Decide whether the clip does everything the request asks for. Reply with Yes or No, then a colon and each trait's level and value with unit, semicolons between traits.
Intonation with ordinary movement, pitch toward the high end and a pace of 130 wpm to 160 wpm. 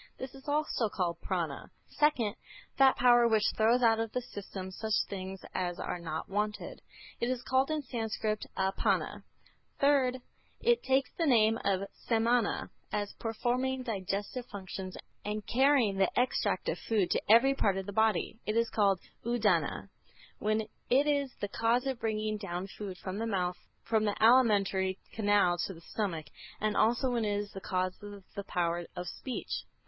No: average, 4.0 semitones; high, 215 Hz; average, 170 wpm